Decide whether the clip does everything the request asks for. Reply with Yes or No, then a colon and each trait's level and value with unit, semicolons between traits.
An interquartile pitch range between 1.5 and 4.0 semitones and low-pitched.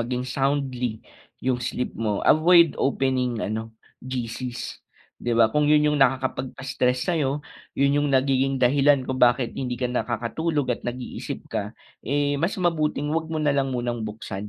Yes: average, 2.9 semitones; low, 130 Hz